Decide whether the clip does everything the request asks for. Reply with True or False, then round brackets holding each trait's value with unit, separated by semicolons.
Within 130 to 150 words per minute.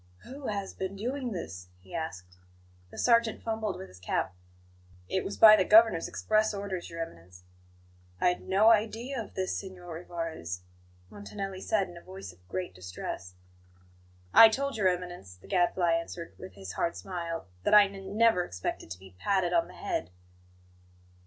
False (170 wpm)